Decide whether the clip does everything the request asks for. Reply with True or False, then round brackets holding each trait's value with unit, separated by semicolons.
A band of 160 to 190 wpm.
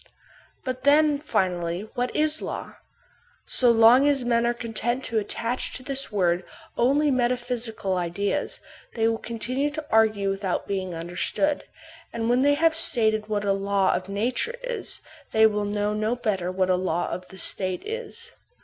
True (165 wpm)